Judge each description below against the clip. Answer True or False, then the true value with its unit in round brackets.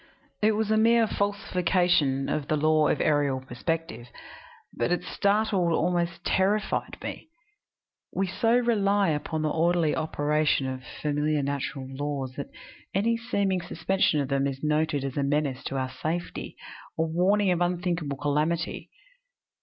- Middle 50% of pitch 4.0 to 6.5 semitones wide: True (4.8 semitones)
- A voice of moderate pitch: True (160 Hz)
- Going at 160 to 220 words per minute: False (145 wpm)